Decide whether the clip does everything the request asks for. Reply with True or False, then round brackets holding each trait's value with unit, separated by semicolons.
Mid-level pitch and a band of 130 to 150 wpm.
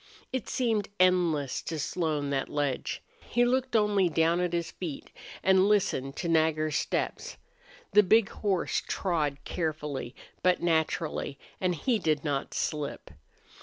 True (170 Hz; 135 wpm)